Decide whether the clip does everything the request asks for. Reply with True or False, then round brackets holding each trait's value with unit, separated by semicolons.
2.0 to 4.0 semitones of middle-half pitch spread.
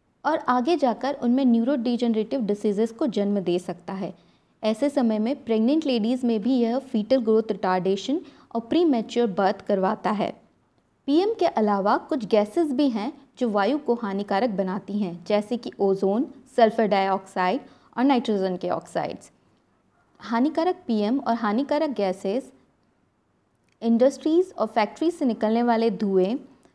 False (4.8 semitones)